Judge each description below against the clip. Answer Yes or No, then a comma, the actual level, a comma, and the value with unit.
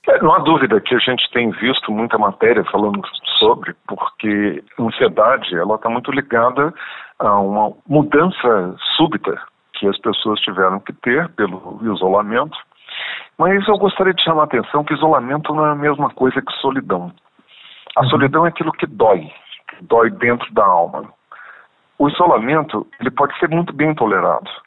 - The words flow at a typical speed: Yes, average, 160 wpm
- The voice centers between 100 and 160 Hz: Yes, medium, 140 Hz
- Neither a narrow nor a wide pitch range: No, wide, 6.7 semitones